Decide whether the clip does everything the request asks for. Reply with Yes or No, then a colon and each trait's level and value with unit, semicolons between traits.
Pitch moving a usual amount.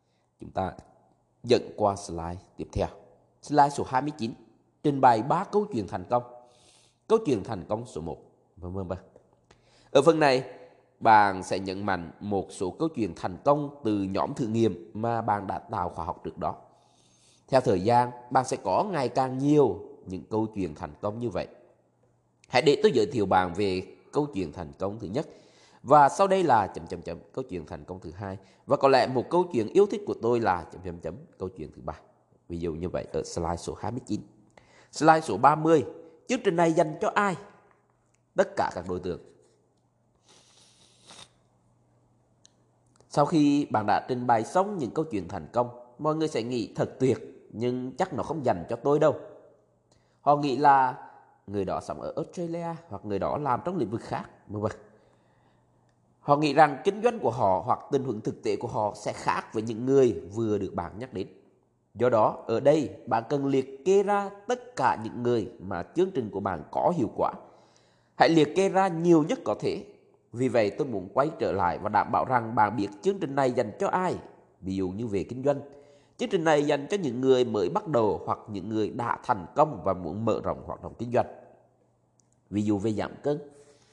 No: wide, 7.0 semitones